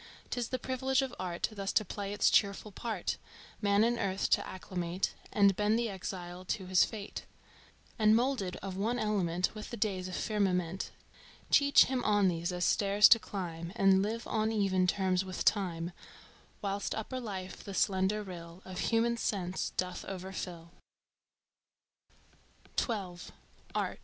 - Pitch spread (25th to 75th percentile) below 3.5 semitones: Yes, average, 2.8 semitones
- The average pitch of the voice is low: No, high, 195 Hz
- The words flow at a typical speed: Yes, average, 145 wpm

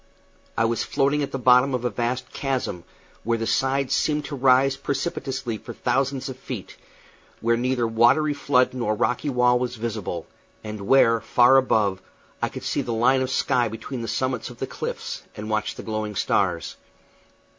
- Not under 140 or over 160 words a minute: No, average, 175 wpm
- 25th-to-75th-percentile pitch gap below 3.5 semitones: Yes, average, 2.9 semitones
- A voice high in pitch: No, low, 125 Hz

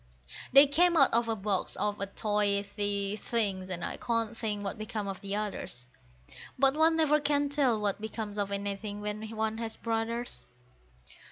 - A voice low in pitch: No, high, 215 Hz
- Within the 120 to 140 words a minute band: No, average, 170 wpm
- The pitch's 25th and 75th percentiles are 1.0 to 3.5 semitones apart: Yes, average, 2.7 semitones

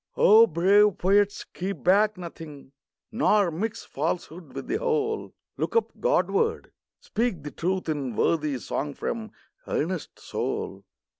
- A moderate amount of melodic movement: No, wide, 5.7 semitones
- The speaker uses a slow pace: Yes, slow, 130 wpm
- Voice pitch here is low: No, high, 190 Hz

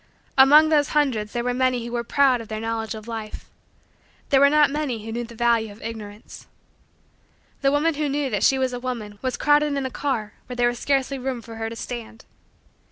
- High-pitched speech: Yes, high, 245 Hz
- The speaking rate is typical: No, fast, 220 wpm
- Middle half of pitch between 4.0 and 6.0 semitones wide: No, average, 3.6 semitones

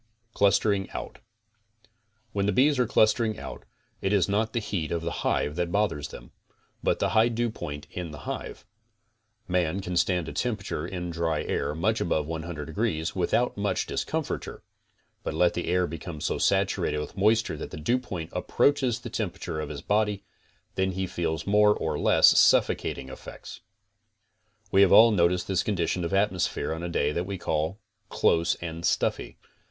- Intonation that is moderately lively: Yes, average, 4.2 semitones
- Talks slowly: No, average, 170 wpm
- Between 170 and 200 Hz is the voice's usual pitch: No, very low, 90 Hz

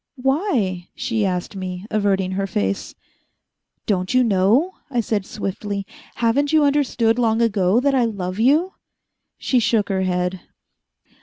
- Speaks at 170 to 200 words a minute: No, average, 140 wpm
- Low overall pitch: No, high, 215 Hz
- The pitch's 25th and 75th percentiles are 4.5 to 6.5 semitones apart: Yes, average, 4.9 semitones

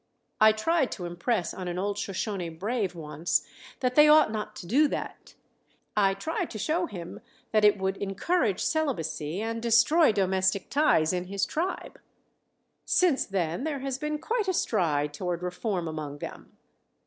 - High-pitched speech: Yes, high, 205 Hz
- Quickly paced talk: No, average, 160 wpm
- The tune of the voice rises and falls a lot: Yes, wide, 7.4 semitones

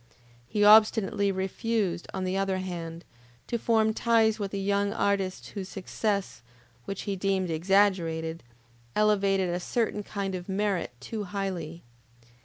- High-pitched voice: Yes, high, 195 Hz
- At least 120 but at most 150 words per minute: Yes, slow, 135 wpm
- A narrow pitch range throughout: Yes, narrow, 2.1 semitones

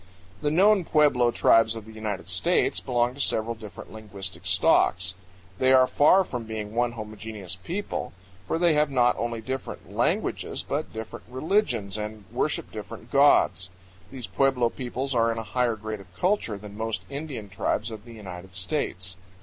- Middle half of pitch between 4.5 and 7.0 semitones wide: No, average, 3.9 semitones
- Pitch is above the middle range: No, low, 115 Hz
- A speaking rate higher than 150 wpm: Yes, average, 165 wpm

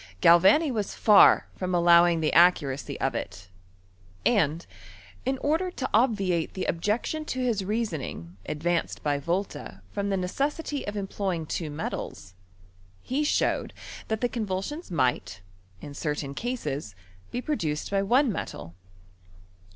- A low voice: No, medium, 185 Hz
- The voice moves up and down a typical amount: No, wide, 7.5 semitones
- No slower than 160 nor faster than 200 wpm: No, slow, 135 wpm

